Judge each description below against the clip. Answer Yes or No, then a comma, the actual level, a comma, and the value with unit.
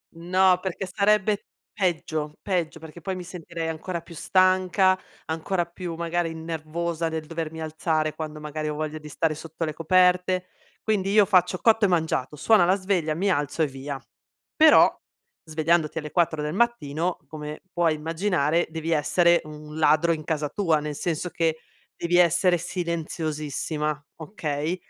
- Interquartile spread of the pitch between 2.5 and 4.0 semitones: Yes, average, 2.8 semitones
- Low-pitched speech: No, medium, 165 Hz